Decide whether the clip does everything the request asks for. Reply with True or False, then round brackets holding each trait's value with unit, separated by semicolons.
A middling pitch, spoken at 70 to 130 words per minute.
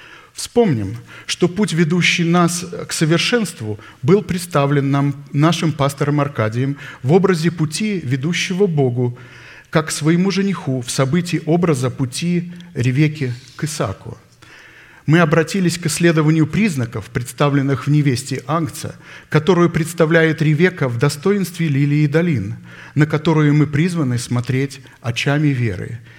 True (155 Hz; 120 wpm)